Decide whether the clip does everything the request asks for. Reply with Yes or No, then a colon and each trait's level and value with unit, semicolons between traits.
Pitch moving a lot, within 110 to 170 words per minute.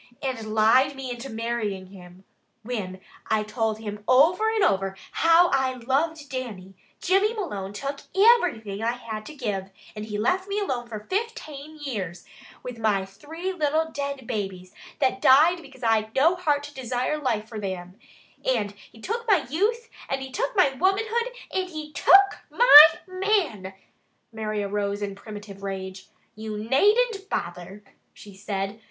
Yes: wide, 7.7 semitones; average, 160 wpm